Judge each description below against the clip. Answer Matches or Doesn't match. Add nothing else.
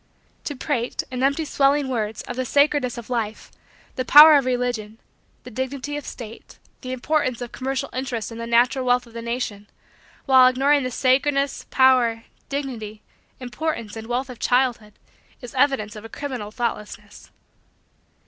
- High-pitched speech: Matches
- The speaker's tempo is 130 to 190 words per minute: Matches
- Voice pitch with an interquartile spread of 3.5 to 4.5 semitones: Doesn't match